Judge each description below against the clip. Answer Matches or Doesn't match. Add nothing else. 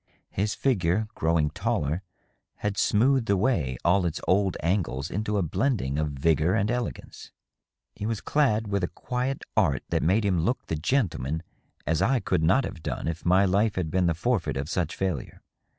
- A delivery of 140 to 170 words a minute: Doesn't match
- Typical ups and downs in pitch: Matches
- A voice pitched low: Matches